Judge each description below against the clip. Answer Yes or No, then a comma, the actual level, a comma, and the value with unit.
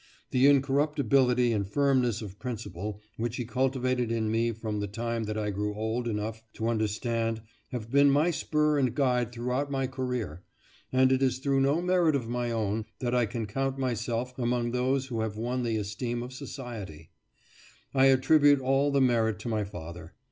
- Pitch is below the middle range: Yes, low, 120 Hz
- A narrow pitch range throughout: No, average, 3.2 semitones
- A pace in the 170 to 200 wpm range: Yes, average, 180 wpm